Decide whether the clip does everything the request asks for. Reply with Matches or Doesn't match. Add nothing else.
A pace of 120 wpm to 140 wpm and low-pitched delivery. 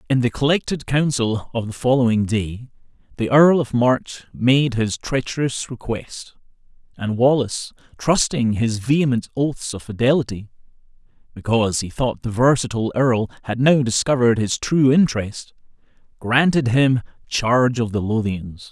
Matches